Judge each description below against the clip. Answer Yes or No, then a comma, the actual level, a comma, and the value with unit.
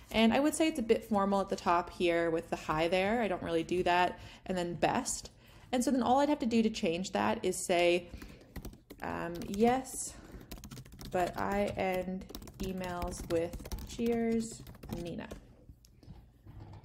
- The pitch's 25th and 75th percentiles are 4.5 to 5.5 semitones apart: Yes, average, 4.8 semitones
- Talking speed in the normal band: Yes, average, 165 wpm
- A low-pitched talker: No, medium, 185 Hz